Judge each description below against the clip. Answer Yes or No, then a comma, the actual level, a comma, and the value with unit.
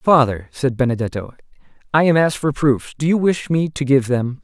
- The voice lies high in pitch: No, medium, 140 Hz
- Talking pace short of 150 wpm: No, fast, 205 wpm